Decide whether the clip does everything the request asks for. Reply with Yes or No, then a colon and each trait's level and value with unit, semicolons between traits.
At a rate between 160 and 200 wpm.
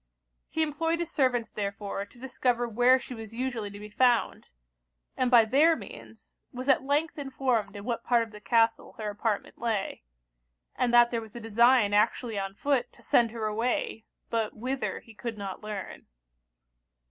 Yes: average, 175 wpm